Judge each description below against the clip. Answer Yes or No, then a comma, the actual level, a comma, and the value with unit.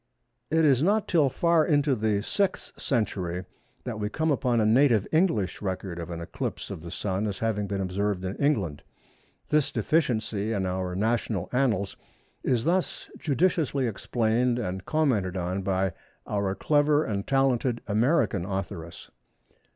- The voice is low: Yes, low, 110 Hz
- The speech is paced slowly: No, average, 150 wpm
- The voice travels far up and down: Yes, wide, 6.4 semitones